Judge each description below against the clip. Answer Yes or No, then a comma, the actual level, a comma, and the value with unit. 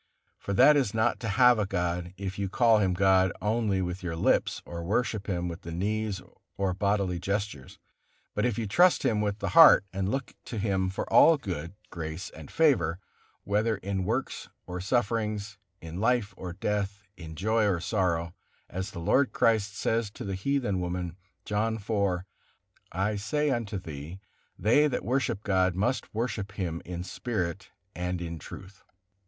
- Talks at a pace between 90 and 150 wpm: No, average, 170 wpm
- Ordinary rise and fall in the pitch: Yes, average, 3.6 semitones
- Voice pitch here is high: No, low, 100 Hz